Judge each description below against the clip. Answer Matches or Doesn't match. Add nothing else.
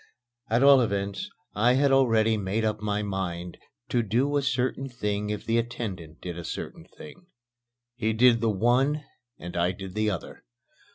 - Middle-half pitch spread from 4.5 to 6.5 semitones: Doesn't match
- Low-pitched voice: Matches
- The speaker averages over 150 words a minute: Matches